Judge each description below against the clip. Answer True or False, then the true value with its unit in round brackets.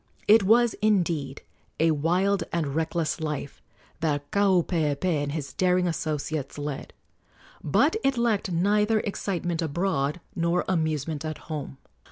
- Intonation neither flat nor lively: True (4.3 semitones)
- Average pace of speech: False (125 wpm)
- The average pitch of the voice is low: False (165 Hz)